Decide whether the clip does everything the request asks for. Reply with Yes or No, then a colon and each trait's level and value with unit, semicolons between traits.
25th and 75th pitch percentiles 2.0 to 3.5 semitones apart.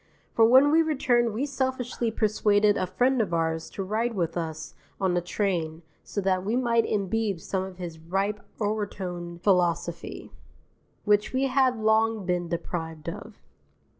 No: average, 4.7 semitones